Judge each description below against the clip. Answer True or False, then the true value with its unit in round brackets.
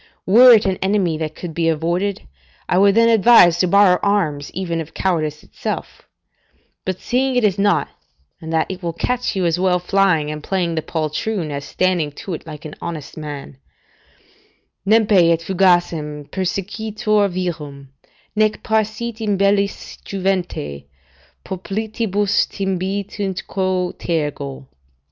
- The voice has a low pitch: False (185 Hz)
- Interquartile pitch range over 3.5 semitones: True (3.9 semitones)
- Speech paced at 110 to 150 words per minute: True (135 wpm)